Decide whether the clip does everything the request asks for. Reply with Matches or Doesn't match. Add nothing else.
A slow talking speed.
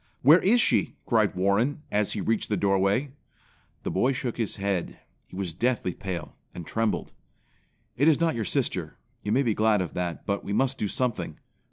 Doesn't match